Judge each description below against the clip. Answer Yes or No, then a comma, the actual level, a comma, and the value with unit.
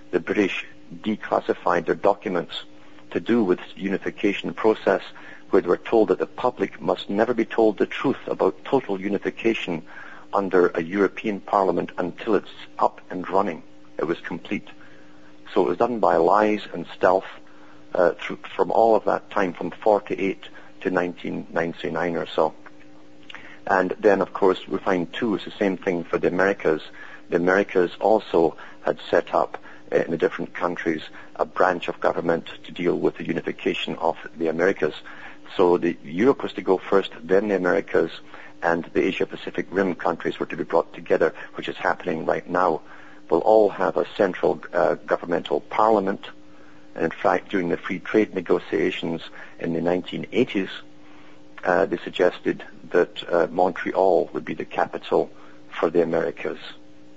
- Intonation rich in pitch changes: Yes, wide, 8.5 semitones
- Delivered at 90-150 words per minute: No, average, 160 wpm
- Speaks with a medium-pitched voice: No, very low, 85 Hz